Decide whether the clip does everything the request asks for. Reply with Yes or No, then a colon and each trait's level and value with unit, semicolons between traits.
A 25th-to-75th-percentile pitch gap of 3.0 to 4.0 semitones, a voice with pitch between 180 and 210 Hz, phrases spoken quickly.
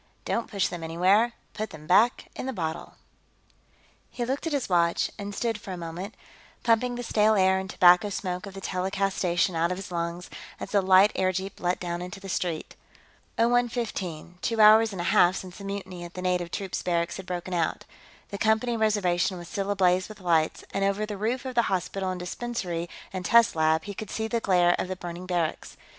Yes: average, 3.4 semitones; high, 190 Hz; fast, 210 wpm